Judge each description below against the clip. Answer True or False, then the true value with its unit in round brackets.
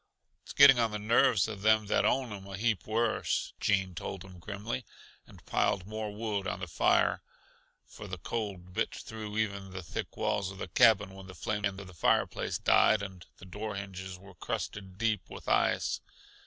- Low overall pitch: True (100 Hz)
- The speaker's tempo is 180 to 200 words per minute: True (190 wpm)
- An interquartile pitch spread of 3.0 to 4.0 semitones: False (2.4 semitones)